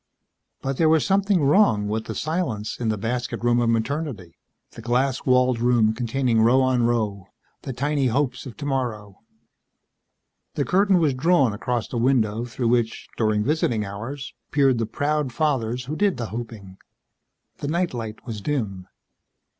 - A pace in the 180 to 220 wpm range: No, average, 160 wpm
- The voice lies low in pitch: Yes, low, 125 Hz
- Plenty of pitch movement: No, average, 4.2 semitones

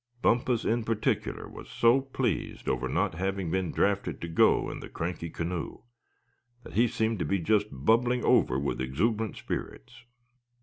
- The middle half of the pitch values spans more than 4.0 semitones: Yes, wide, 5.6 semitones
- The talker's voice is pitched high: No, low, 105 Hz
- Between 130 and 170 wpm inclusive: Yes, average, 160 wpm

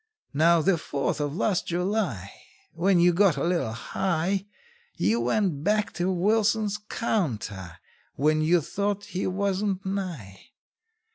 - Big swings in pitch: No, average, 5.0 semitones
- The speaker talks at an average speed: No, slow, 130 wpm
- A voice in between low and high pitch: Yes, medium, 180 Hz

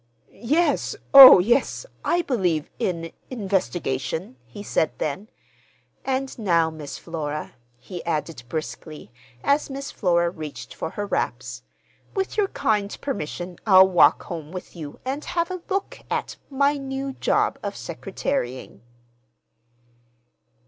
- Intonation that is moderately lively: No, wide, 9.0 semitones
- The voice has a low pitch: No, high, 190 Hz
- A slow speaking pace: Yes, slow, 120 wpm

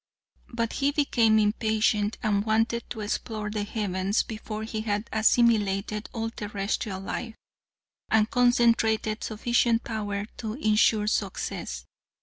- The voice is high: Yes, high, 220 Hz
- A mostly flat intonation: Yes, narrow, 1.6 semitones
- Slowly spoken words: Yes, slow, 120 wpm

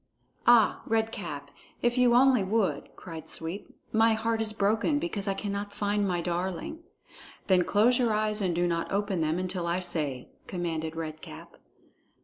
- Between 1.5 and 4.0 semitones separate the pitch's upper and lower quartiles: No, average, 4.4 semitones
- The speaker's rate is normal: Yes, average, 165 wpm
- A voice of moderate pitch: No, high, 200 Hz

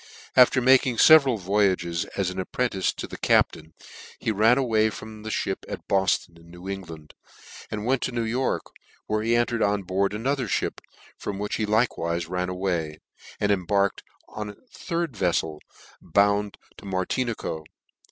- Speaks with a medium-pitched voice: No, low, 100 Hz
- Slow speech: No, average, 160 wpm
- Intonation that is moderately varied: Yes, average, 4.1 semitones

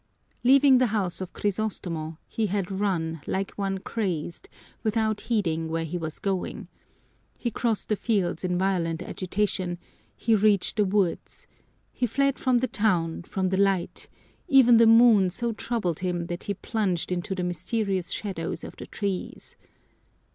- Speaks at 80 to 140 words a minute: No, average, 155 wpm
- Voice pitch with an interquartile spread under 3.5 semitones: No, average, 3.8 semitones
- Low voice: No, high, 195 Hz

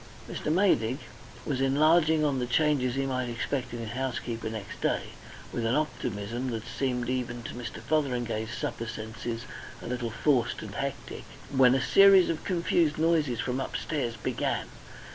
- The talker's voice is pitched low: Yes, low, 125 Hz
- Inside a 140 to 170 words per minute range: Yes, average, 160 wpm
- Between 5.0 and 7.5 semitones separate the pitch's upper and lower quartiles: No, average, 4.1 semitones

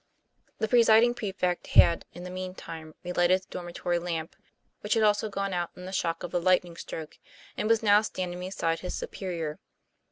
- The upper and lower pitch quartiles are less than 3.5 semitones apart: Yes, average, 2.8 semitones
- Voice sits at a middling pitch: Yes, medium, 180 Hz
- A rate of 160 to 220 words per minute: Yes, average, 190 wpm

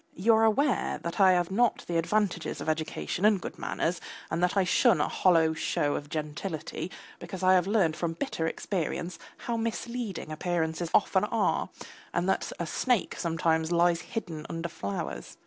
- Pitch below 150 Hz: No, medium, 175 Hz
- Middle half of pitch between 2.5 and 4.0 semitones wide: Yes, average, 3.6 semitones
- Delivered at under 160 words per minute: No, average, 170 wpm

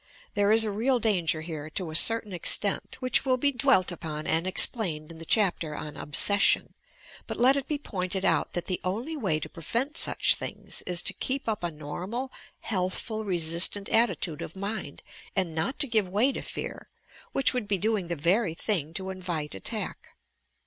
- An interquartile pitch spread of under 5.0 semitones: No, average, 5.3 semitones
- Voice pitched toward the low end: No, high, 190 Hz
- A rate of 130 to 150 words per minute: No, average, 185 wpm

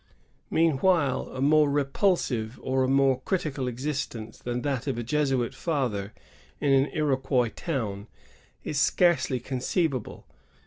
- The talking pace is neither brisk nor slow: No, slow, 130 wpm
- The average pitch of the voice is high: No, low, 135 Hz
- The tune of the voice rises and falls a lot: No, average, 3.2 semitones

